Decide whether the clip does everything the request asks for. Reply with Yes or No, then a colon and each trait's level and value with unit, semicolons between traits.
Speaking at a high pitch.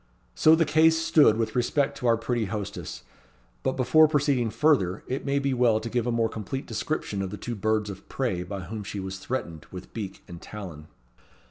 No: low, 115 Hz